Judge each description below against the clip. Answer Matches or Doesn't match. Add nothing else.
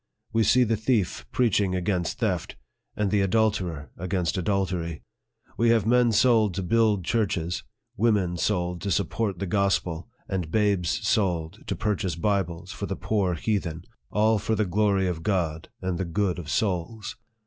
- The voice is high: Doesn't match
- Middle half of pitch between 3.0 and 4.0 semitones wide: Matches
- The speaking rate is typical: Matches